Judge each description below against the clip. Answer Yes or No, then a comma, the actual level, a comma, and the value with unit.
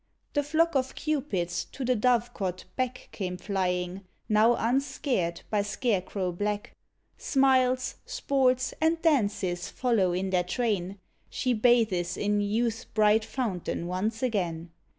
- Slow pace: Yes, slow, 125 wpm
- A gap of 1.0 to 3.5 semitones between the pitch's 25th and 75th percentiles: No, wide, 5.5 semitones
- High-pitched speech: Yes, high, 215 Hz